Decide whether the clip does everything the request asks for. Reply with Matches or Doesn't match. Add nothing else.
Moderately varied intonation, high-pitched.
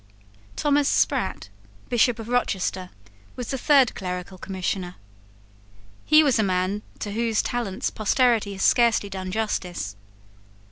Matches